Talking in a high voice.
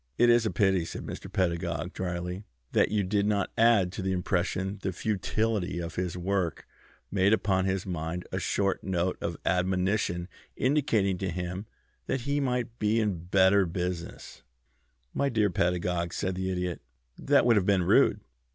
No: very low, 95 Hz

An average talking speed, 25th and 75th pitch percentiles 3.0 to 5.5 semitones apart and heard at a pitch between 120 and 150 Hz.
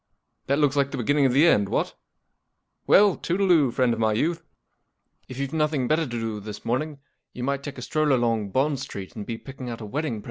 No: fast, 225 wpm; average, 4.5 semitones; low, 135 Hz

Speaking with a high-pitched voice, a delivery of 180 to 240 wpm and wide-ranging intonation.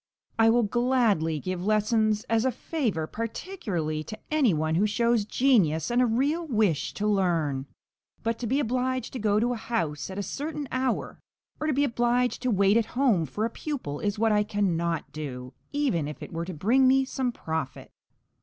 Yes: high, 220 Hz; average, 190 wpm; wide, 6.6 semitones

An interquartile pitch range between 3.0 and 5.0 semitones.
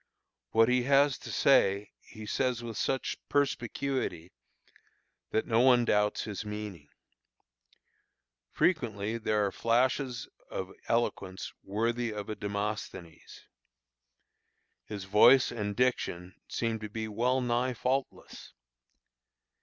Yes: average, 3.5 semitones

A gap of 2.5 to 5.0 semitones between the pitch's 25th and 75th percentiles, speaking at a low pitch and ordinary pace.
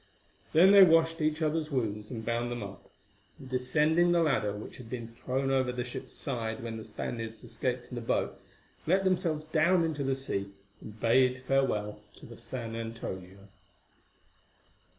No: wide, 5.4 semitones; low, 125 Hz; average, 170 wpm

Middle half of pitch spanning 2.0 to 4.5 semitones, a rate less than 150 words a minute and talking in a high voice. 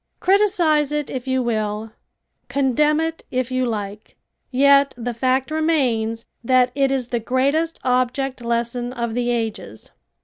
Yes: average, 3.1 semitones; average, 140 wpm; very high, 255 Hz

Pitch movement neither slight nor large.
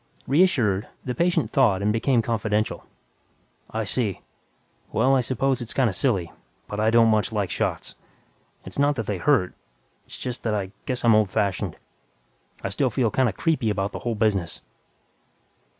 Yes: average, 3.9 semitones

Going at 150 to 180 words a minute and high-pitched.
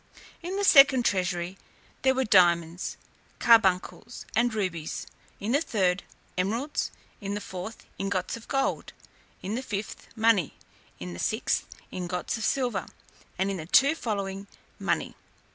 No: average, 140 wpm; high, 200 Hz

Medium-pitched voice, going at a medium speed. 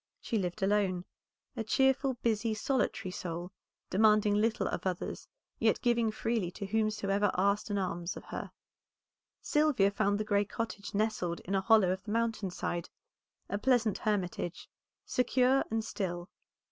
No: high, 210 Hz; average, 145 wpm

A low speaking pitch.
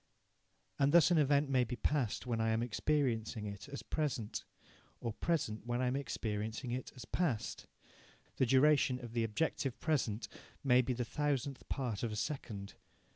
Yes: low, 125 Hz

